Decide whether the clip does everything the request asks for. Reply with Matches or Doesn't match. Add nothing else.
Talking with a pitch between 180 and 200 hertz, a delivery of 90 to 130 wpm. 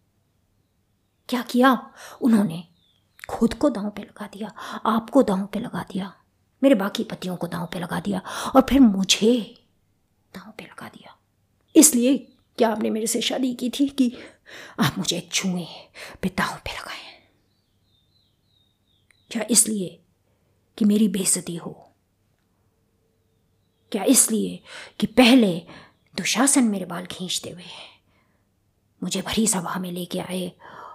Matches